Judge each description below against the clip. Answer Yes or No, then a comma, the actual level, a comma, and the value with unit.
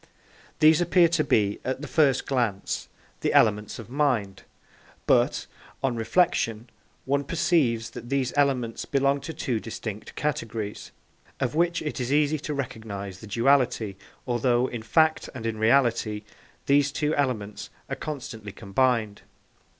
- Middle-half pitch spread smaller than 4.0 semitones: No, average, 4.5 semitones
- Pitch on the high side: No, low, 125 Hz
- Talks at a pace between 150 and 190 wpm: No, average, 140 wpm